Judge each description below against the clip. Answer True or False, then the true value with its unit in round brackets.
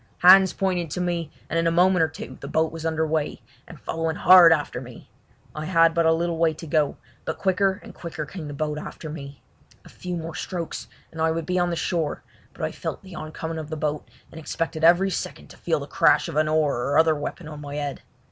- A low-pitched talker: False (160 Hz)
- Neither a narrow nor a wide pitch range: False (2.0 semitones)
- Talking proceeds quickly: True (240 wpm)